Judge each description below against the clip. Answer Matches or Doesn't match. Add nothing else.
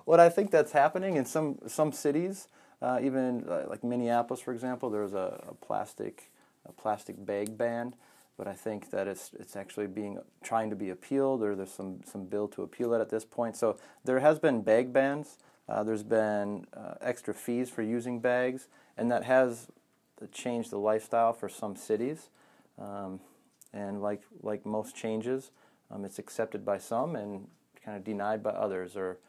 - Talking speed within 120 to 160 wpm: Doesn't match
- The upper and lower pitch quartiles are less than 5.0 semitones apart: Matches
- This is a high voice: Doesn't match